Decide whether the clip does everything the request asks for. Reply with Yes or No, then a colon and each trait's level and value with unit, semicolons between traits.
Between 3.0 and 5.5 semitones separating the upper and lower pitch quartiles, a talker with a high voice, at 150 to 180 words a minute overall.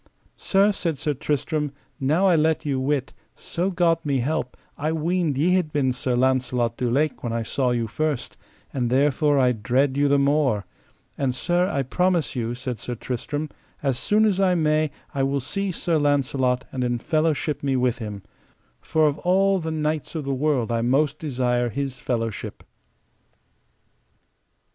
No: average, 3.9 semitones; medium, 140 Hz; average, 170 wpm